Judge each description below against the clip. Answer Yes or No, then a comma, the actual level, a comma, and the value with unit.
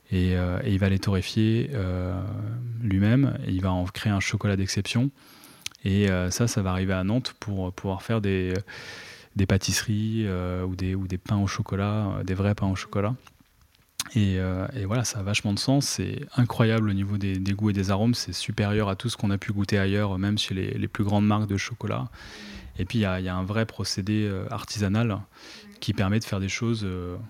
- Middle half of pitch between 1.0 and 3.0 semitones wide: Yes, average, 2.7 semitones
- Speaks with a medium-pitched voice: No, low, 100 Hz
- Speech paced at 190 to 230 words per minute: Yes, fast, 220 wpm